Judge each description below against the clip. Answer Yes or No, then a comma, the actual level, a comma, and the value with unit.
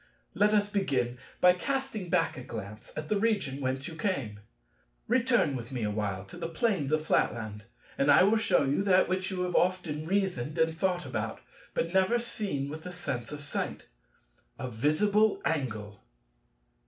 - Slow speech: No, average, 170 wpm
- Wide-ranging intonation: Yes, wide, 7.7 semitones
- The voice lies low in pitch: No, medium, 155 Hz